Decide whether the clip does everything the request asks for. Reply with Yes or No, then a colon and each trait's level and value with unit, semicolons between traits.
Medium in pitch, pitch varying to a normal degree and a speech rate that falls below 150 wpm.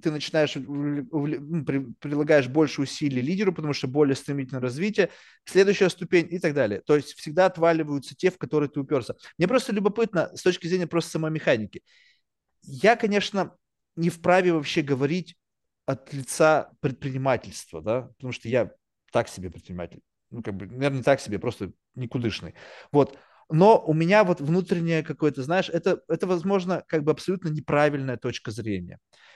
No: medium, 150 Hz; average, 4.6 semitones; average, 155 wpm